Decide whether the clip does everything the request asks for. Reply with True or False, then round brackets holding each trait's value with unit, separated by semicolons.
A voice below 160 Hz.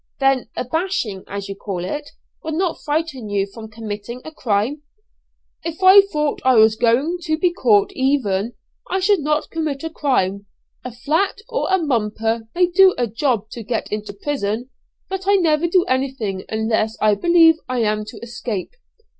False (255 Hz)